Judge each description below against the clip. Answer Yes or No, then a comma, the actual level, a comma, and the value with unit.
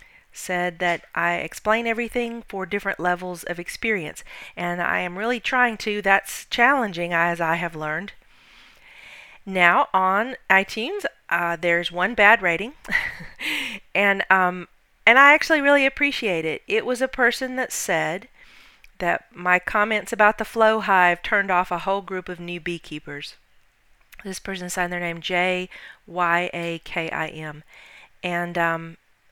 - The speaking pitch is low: No, high, 190 Hz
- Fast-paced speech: No, average, 145 wpm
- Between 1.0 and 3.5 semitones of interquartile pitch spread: No, average, 4.5 semitones